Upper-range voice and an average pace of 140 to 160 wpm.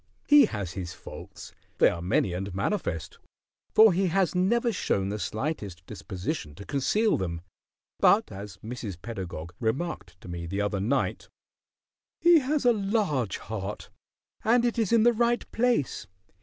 No: low, 115 Hz; average, 155 wpm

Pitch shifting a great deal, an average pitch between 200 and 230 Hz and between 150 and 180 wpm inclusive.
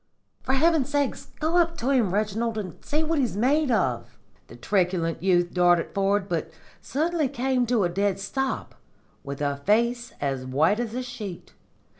Yes: wide, 6.9 semitones; high, 220 Hz; average, 170 wpm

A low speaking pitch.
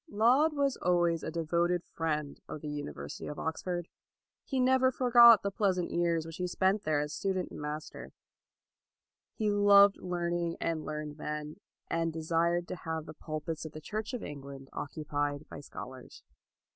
No: medium, 170 Hz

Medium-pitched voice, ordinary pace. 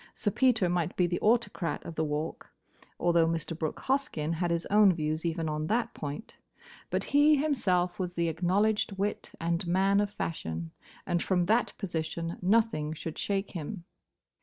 Yes: medium, 175 Hz; average, 165 wpm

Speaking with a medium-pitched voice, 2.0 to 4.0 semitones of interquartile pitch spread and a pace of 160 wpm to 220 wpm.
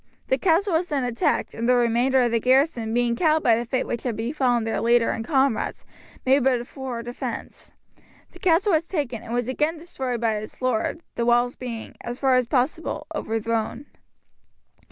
No: high, 245 Hz; average, 3.2 semitones; average, 190 wpm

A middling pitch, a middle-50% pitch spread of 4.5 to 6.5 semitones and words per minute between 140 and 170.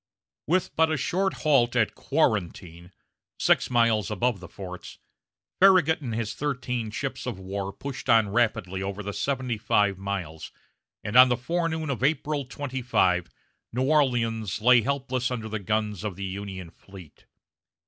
No: low, 115 Hz; average, 5.3 semitones; average, 150 wpm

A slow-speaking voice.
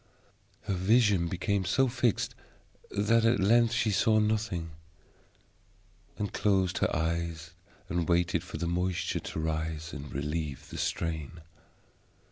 Yes: slow, 125 wpm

